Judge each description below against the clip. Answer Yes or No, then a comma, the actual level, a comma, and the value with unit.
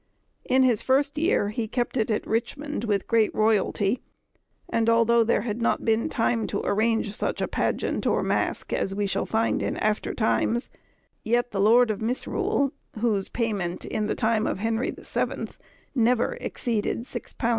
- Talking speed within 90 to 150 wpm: No, average, 175 wpm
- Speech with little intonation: Yes, narrow, 2.1 semitones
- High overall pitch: Yes, high, 225 Hz